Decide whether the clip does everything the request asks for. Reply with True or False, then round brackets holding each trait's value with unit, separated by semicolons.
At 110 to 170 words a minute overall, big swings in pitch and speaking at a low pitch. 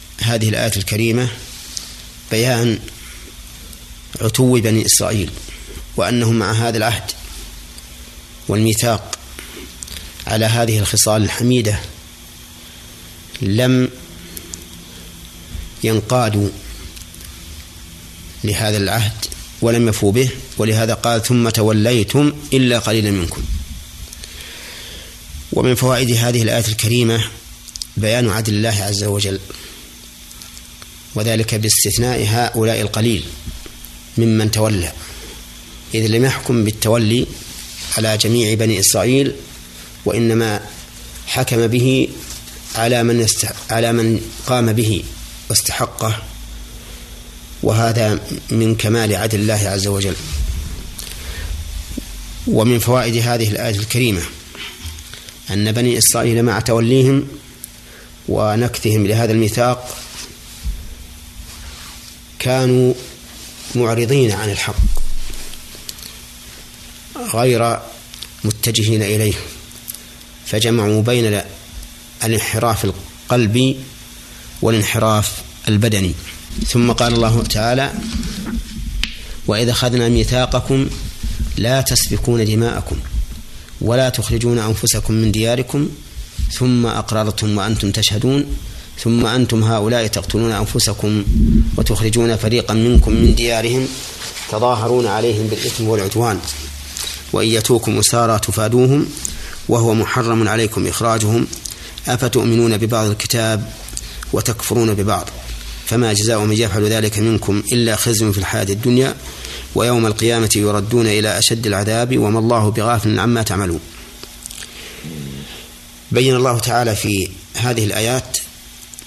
False (85 wpm; 6.1 semitones; 110 Hz)